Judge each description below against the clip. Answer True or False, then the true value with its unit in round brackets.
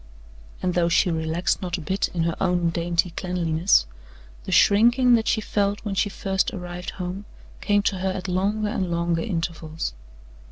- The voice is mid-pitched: True (180 Hz)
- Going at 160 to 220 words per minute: True (170 wpm)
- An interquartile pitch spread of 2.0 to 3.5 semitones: True (2.9 semitones)